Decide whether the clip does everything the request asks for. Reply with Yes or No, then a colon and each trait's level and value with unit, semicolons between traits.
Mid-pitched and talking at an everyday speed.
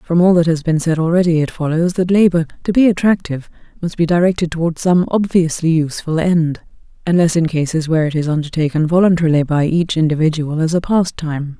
Yes: medium, 165 Hz; average, 185 wpm